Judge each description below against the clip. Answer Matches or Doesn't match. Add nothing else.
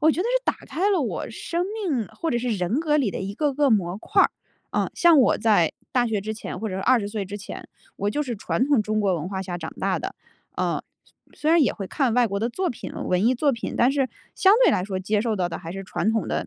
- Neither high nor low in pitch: Doesn't match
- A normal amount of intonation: Doesn't match